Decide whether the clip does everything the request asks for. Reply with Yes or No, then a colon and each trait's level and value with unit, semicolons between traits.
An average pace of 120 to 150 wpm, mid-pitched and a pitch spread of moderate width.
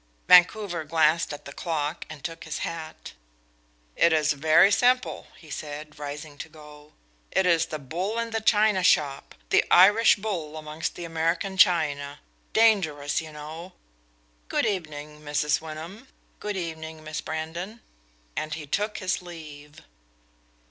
Yes: average, 140 wpm; medium, 160 Hz; average, 3.5 semitones